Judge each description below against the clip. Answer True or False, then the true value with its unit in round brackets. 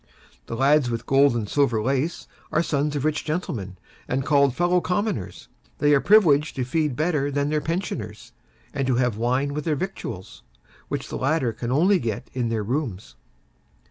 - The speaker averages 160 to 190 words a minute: True (175 wpm)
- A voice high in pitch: False (140 Hz)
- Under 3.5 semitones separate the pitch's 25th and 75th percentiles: False (4.3 semitones)